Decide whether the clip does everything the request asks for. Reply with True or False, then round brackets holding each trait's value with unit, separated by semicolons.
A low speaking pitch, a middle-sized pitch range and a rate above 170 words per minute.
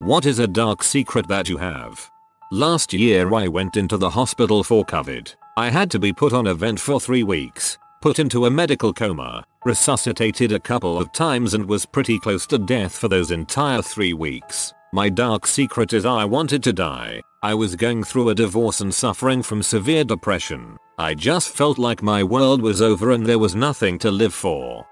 True (115 Hz; 4.1 semitones; 200 wpm)